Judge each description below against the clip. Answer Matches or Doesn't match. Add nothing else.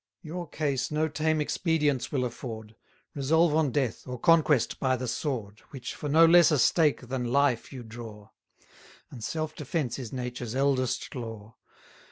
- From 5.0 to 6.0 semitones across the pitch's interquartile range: Doesn't match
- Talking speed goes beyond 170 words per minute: Doesn't match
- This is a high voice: Doesn't match